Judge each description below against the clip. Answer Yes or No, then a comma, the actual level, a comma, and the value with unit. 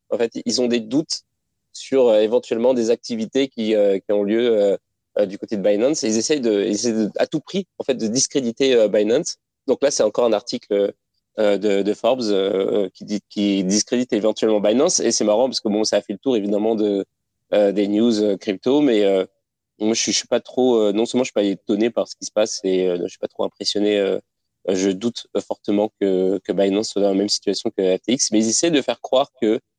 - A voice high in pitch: No, low, 105 Hz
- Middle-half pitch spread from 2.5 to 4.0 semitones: Yes, average, 3.7 semitones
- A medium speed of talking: No, fast, 240 wpm